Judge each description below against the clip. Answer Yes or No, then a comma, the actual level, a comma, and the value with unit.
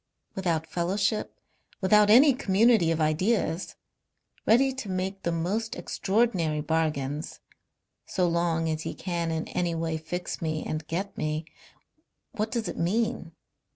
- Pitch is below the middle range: No, medium, 175 Hz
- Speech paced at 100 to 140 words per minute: Yes, slow, 135 wpm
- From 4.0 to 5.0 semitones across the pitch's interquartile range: Yes, average, 4.6 semitones